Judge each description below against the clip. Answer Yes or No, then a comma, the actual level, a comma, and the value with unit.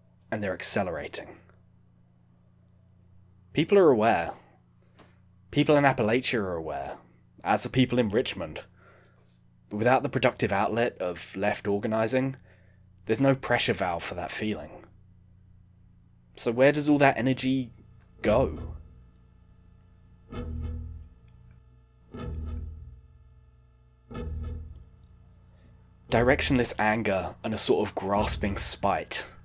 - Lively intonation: Yes, wide, 5.9 semitones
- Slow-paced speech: Yes, slow, 95 wpm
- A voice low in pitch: Yes, very low, 95 Hz